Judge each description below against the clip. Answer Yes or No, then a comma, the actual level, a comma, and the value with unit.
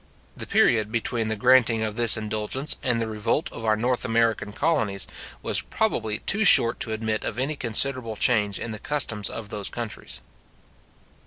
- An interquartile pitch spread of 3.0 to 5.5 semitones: No, narrow, 2.4 semitones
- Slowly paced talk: No, average, 170 wpm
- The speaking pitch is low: Yes, low, 115 Hz